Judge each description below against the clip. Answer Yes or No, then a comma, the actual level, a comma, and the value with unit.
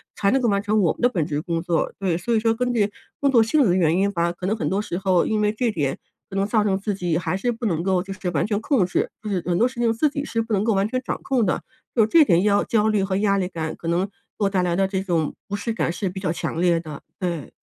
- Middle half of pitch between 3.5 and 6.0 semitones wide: Yes, average, 3.8 semitones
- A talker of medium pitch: No, high, 195 Hz